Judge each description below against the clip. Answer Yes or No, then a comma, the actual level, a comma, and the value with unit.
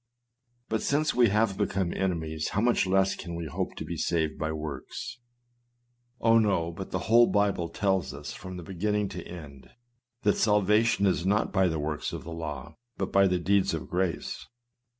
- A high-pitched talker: No, very low, 95 Hz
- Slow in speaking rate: No, average, 185 wpm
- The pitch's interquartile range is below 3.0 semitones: No, average, 3.8 semitones